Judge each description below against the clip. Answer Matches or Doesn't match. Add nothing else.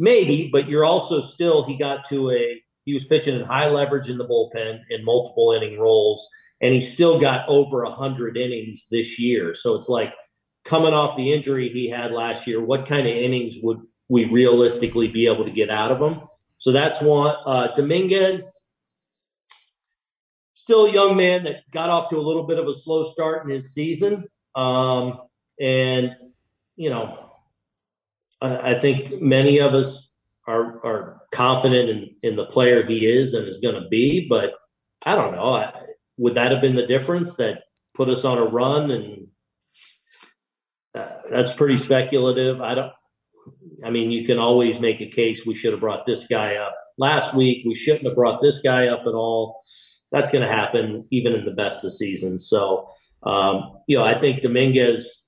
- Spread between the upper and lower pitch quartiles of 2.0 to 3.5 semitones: Doesn't match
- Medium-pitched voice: Doesn't match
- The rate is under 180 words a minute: Doesn't match